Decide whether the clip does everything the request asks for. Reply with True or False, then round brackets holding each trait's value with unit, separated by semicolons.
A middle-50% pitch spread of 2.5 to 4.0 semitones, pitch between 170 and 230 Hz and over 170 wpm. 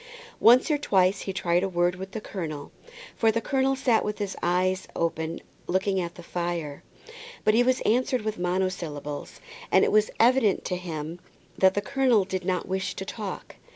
True (3.6 semitones; 190 Hz; 185 wpm)